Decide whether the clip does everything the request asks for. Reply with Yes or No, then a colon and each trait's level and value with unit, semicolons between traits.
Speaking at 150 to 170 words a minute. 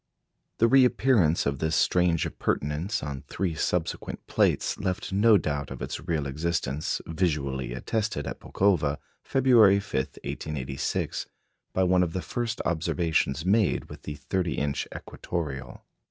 No: slow, 135 wpm